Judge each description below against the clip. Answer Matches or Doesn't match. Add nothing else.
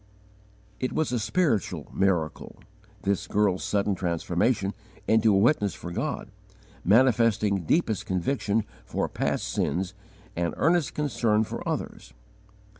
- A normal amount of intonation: Matches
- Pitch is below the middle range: Matches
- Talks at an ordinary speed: Doesn't match